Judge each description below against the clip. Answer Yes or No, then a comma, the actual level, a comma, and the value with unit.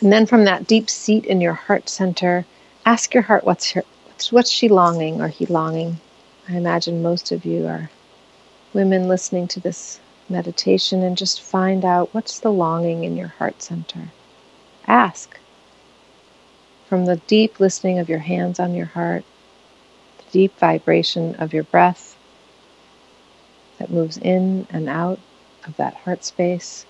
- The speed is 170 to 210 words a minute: No, average, 155 wpm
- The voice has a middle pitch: Yes, medium, 180 Hz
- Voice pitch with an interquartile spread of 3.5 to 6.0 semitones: No, narrow, 2.5 semitones